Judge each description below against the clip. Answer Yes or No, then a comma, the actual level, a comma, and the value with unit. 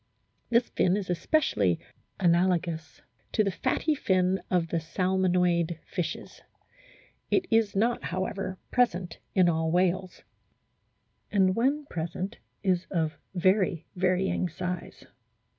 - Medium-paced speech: No, slow, 110 wpm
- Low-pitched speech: No, medium, 185 Hz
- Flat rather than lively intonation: Yes, narrow, 2.2 semitones